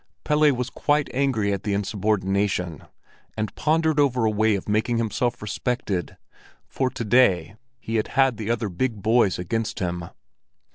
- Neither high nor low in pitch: No, low, 110 Hz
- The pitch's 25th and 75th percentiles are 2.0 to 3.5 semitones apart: No, average, 4.1 semitones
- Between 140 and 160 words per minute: Yes, average, 155 wpm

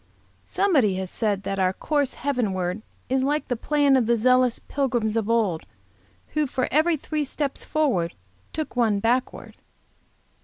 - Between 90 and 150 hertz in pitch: No, very high, 250 Hz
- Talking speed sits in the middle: Yes, average, 150 wpm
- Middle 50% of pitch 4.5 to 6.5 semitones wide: Yes, average, 5.2 semitones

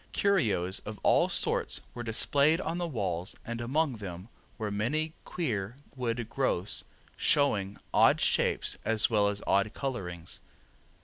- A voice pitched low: Yes, low, 115 Hz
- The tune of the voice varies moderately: No, wide, 5.8 semitones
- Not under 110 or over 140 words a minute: Yes, slow, 135 wpm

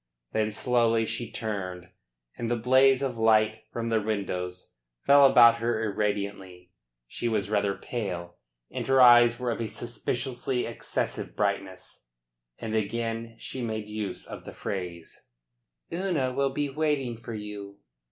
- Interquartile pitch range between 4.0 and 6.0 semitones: No, average, 3.0 semitones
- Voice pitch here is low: Yes, low, 115 Hz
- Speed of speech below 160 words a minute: Yes, average, 140 wpm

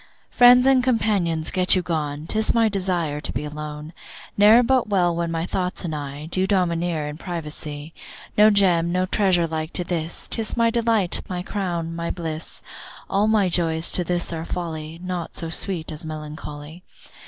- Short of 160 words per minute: No, average, 175 wpm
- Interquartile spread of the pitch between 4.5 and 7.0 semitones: No, average, 3.7 semitones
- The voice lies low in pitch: No, medium, 170 Hz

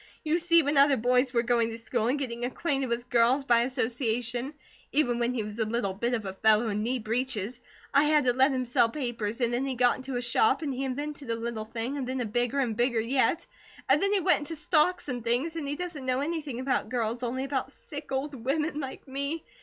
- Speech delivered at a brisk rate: Yes, fast, 240 wpm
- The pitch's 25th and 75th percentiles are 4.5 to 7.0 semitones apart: No, average, 3.2 semitones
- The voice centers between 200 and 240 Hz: No, very high, 255 Hz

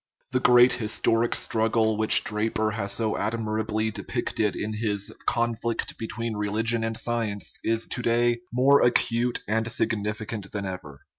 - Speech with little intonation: Yes, narrow, 1.7 semitones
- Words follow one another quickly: No, average, 150 wpm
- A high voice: No, low, 110 Hz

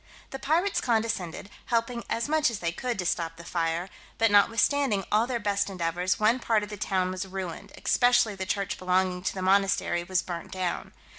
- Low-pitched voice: No, high, 195 Hz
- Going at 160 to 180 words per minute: No, average, 195 wpm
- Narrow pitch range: No, average, 4.1 semitones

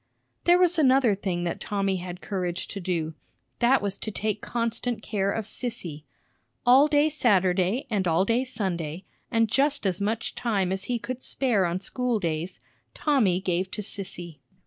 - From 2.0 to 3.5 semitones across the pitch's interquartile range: No, average, 5.1 semitones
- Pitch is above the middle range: Yes, high, 200 Hz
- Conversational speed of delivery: Yes, average, 170 wpm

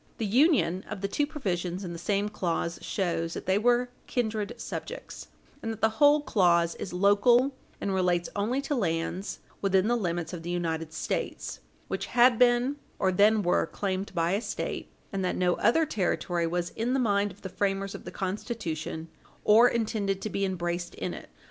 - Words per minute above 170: Yes, average, 185 wpm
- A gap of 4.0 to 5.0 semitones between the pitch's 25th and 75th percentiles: Yes, average, 4.5 semitones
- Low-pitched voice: No, high, 195 Hz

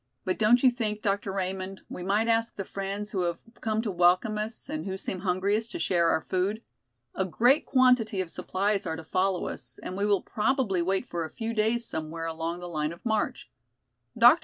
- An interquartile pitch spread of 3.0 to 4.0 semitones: Yes, average, 3.7 semitones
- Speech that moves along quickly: Yes, fast, 210 wpm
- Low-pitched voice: No, high, 195 Hz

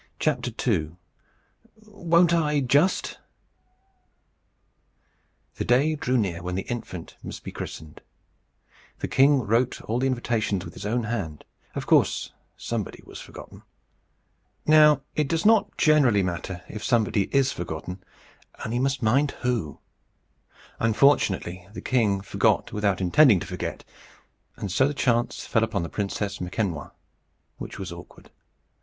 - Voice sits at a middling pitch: No, low, 115 Hz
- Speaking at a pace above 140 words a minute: No, slow, 135 wpm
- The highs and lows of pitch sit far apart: Yes, wide, 6.5 semitones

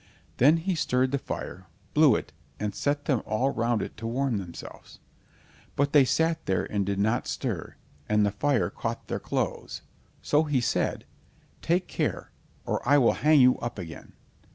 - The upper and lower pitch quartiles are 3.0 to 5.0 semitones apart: No, wide, 5.4 semitones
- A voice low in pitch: Yes, low, 125 Hz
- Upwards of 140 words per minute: Yes, average, 175 wpm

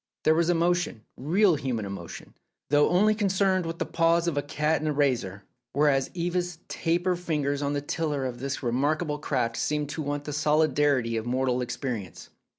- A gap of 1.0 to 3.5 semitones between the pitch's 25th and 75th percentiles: No, average, 4.3 semitones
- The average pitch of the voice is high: No, medium, 150 Hz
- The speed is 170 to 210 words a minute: Yes, average, 175 wpm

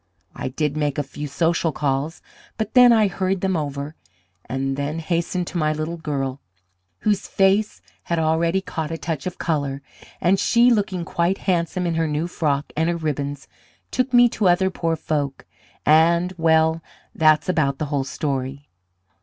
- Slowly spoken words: No, average, 170 wpm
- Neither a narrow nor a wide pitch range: Yes, average, 3.7 semitones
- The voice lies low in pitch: No, medium, 160 Hz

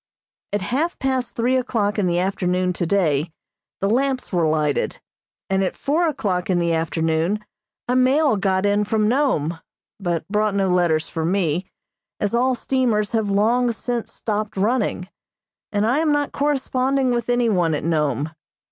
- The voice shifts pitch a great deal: Yes, wide, 5.9 semitones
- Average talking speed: Yes, average, 160 wpm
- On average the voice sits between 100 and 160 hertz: No, high, 205 Hz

